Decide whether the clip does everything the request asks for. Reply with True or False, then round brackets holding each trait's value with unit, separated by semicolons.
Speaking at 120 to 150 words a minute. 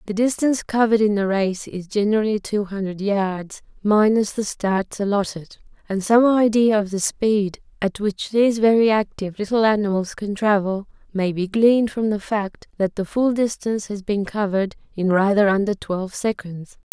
False (170 wpm)